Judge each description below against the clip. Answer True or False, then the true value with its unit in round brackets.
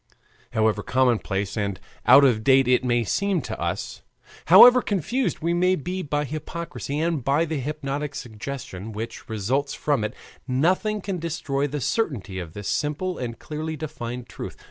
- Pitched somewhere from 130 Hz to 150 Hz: True (140 Hz)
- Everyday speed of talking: True (160 wpm)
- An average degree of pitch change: False (5.8 semitones)